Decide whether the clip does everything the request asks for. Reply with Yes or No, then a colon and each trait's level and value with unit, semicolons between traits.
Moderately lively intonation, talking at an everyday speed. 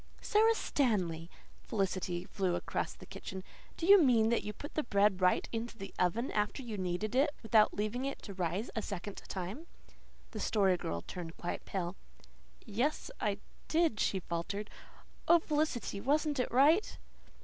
No: wide, 6.3 semitones; average, 160 wpm